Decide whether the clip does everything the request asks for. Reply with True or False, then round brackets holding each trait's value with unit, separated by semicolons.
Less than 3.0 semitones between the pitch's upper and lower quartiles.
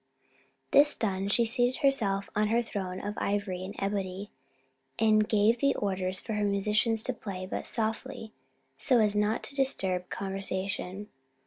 True (2.5 semitones)